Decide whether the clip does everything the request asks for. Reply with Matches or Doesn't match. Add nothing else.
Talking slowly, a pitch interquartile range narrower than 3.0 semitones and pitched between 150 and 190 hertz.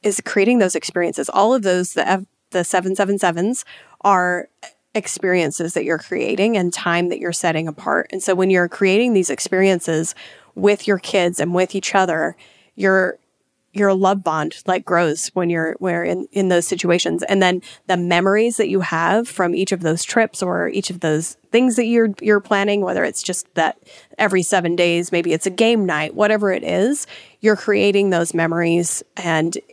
Doesn't match